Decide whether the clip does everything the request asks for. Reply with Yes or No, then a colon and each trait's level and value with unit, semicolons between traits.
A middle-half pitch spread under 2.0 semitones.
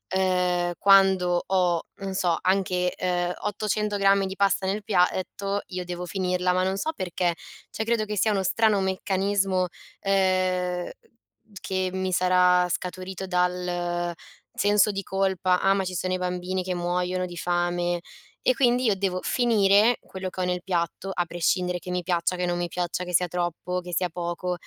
Yes: narrow, 1.5 semitones